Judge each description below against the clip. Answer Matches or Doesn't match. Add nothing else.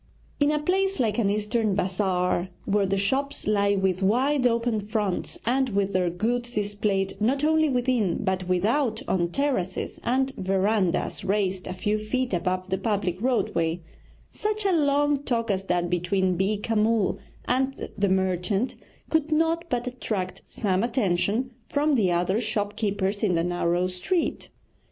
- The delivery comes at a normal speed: Matches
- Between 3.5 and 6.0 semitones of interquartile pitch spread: Matches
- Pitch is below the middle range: Doesn't match